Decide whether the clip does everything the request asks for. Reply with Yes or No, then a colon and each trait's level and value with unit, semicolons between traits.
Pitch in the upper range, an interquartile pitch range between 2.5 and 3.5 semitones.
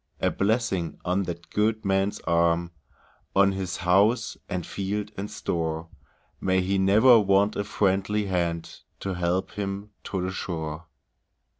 No: very low, 95 Hz; average, 2.8 semitones